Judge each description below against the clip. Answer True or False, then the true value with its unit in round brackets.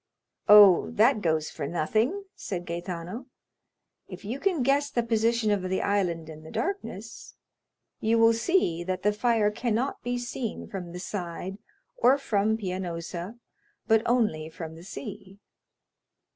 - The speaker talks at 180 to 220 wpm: False (145 wpm)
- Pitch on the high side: True (205 Hz)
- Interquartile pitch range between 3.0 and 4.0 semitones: False (5.1 semitones)